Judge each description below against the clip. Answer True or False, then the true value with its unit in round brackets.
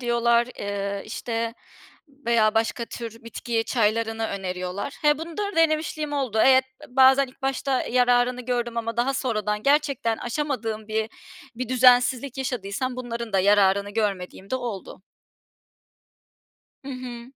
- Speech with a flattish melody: False (3.0 semitones)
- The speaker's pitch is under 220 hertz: False (235 Hz)